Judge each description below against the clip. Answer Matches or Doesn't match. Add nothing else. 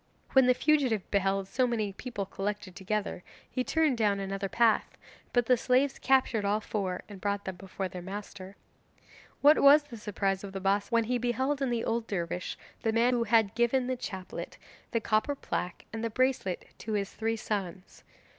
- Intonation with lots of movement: Doesn't match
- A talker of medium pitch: Doesn't match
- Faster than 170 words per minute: Matches